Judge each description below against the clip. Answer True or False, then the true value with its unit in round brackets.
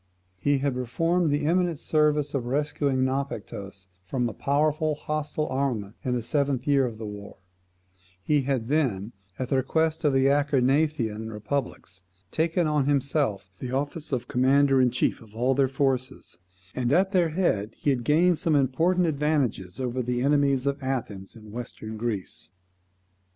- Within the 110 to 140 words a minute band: False (160 wpm)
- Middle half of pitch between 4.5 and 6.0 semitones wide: False (3.7 semitones)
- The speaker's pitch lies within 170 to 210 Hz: False (135 Hz)